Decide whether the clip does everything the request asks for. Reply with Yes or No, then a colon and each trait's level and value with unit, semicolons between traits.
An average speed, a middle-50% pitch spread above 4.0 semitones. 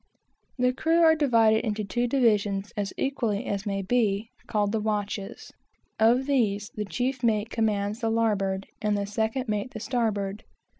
No: average, 160 wpm; average, 3.0 semitones